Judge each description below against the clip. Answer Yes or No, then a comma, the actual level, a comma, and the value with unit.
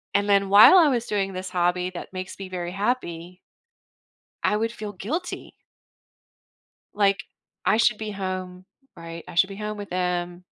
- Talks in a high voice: Yes, high, 195 Hz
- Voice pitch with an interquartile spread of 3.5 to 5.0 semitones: No, average, 2.7 semitones